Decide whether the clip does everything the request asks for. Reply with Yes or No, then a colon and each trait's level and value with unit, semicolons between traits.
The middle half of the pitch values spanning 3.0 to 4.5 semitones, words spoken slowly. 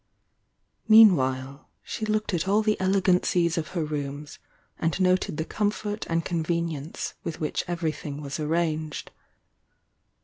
Yes: average, 3.7 semitones; slow, 130 wpm